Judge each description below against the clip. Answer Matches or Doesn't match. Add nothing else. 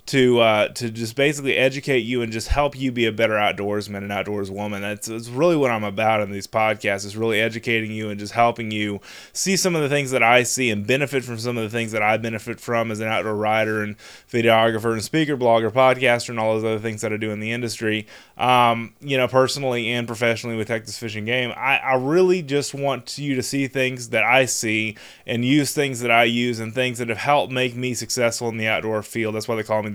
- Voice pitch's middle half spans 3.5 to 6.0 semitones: Doesn't match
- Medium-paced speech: Doesn't match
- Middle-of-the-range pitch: Doesn't match